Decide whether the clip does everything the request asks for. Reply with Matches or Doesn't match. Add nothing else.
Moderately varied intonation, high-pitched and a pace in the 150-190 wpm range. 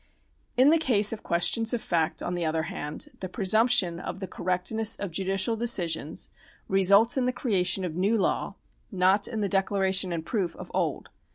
Matches